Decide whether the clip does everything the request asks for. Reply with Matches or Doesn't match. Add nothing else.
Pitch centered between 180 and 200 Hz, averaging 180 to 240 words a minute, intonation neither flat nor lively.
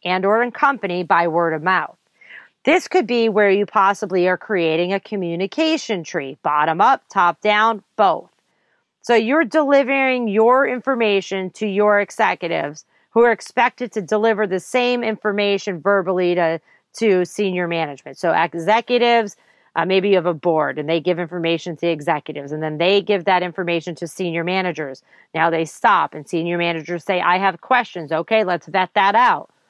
Doesn't match